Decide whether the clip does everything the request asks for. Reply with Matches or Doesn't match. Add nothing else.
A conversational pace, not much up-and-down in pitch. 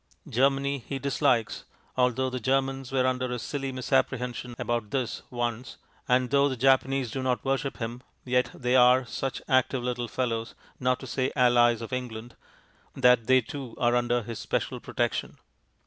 Matches